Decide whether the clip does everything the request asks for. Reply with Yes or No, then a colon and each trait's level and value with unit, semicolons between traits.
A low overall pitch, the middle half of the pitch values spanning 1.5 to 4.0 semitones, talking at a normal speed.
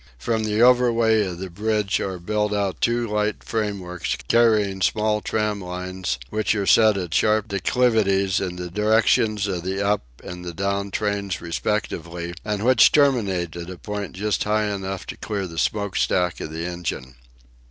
Yes: low, 100 Hz; average, 3.0 semitones; average, 170 wpm